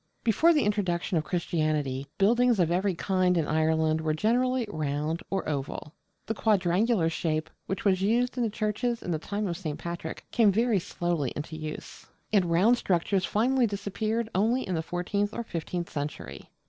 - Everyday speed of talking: Yes, average, 175 wpm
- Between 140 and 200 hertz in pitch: Yes, medium, 185 Hz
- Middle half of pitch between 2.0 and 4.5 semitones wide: No, average, 5.2 semitones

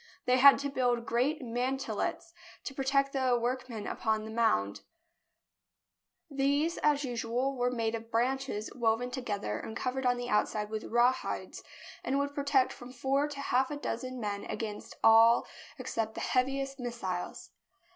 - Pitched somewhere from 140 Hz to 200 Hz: No, very high, 250 Hz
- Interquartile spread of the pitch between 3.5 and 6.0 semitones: No, average, 3.1 semitones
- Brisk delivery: No, average, 160 wpm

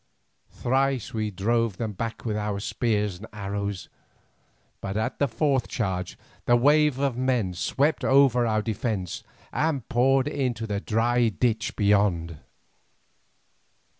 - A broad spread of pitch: No, average, 4.0 semitones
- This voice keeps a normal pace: No, slow, 130 wpm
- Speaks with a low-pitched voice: Yes, low, 115 Hz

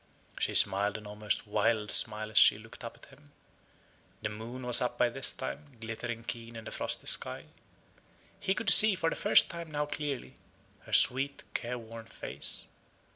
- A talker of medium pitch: No, low, 115 Hz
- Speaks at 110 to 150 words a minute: No, average, 175 wpm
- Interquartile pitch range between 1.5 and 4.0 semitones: No, average, 4.4 semitones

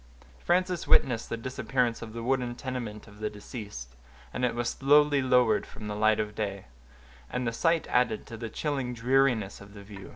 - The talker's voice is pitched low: Yes, low, 115 Hz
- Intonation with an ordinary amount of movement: Yes, average, 3.3 semitones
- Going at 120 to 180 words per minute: No, average, 190 wpm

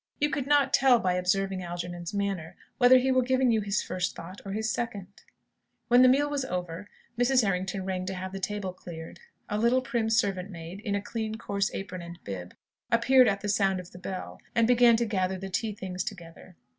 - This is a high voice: Yes, high, 200 Hz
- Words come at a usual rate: No, fast, 210 wpm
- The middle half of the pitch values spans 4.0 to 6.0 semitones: Yes, average, 4.3 semitones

